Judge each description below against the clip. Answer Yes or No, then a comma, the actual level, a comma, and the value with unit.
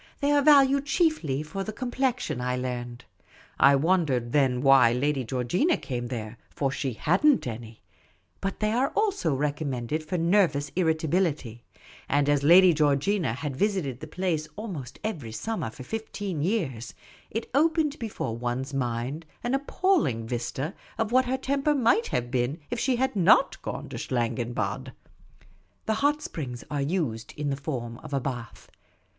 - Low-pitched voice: No, medium, 150 Hz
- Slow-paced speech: No, average, 165 wpm